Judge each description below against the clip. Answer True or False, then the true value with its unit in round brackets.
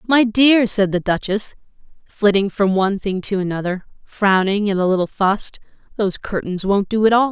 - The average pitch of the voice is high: True (200 Hz)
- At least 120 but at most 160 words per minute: False (180 wpm)